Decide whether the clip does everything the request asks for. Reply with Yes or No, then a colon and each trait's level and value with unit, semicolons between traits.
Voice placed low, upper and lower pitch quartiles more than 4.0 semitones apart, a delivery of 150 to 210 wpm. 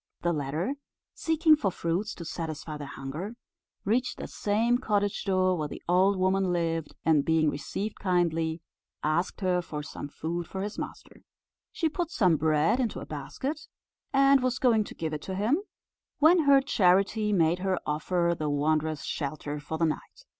No: medium, 180 Hz; average, 5.2 semitones; average, 170 wpm